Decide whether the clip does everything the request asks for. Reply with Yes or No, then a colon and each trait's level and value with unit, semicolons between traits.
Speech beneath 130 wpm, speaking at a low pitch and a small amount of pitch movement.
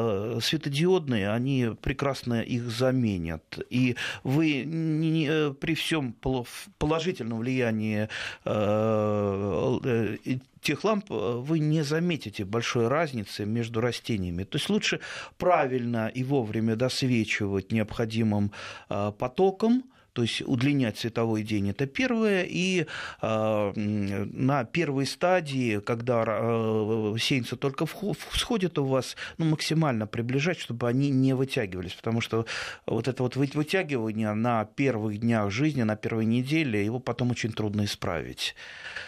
No: average, 115 wpm; low, 120 Hz; average, 4.9 semitones